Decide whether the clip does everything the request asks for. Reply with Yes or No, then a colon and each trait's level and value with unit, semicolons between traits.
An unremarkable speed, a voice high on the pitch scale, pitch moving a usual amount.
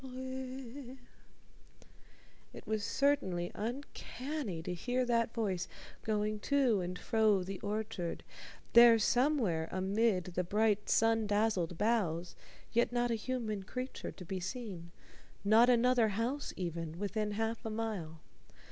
No: slow, 125 wpm; high, 220 Hz; average, 4.4 semitones